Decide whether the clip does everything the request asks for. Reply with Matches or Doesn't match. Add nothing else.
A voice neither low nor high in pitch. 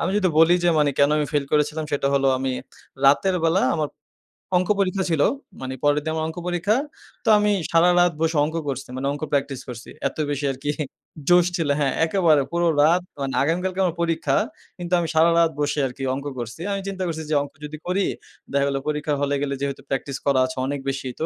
Matches